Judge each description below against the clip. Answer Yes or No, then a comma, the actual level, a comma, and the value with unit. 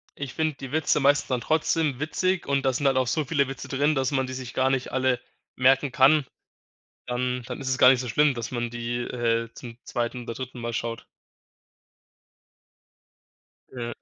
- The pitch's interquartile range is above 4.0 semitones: No, narrow, 2.5 semitones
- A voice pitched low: Yes, low, 130 Hz